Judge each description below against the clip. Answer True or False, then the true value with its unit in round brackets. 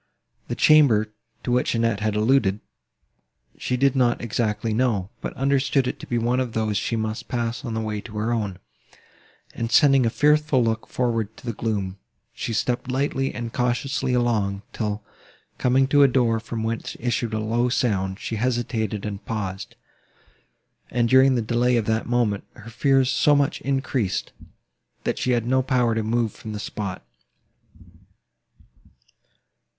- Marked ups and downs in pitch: False (2.6 semitones)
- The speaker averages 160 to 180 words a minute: True (165 wpm)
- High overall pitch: False (115 Hz)